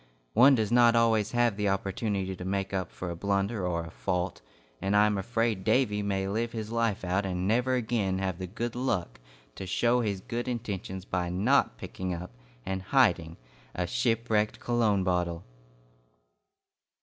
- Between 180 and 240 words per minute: No, average, 170 wpm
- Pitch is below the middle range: Yes, low, 100 Hz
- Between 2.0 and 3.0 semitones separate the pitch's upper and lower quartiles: No, average, 3.9 semitones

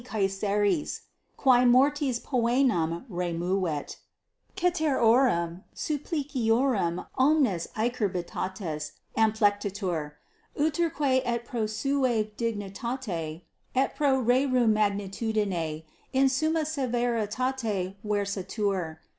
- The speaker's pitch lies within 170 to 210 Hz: No, high, 225 Hz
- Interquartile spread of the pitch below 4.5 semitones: No, average, 5.3 semitones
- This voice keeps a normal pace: No, slow, 70 wpm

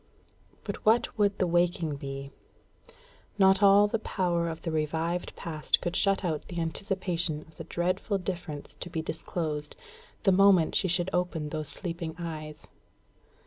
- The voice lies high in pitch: No, medium, 170 Hz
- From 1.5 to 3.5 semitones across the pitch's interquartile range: Yes, average, 3.1 semitones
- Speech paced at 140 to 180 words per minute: Yes, average, 150 wpm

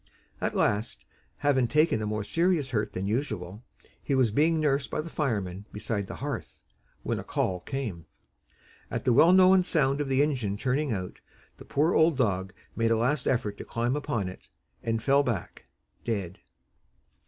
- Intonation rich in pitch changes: Yes, wide, 5.8 semitones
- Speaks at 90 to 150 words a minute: No, average, 175 wpm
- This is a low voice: Yes, low, 125 Hz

